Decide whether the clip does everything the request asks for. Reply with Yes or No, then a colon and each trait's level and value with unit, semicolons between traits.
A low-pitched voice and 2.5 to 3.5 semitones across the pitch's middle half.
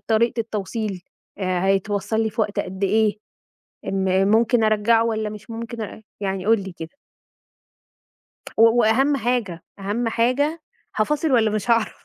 No: high, 220 Hz; average, 2.8 semitones